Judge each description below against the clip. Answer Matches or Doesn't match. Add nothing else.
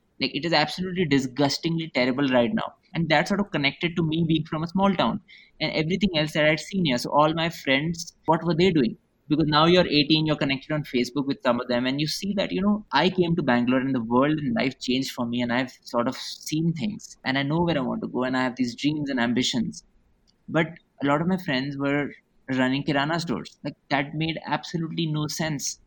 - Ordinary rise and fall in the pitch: Matches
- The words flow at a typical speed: Doesn't match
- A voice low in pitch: Doesn't match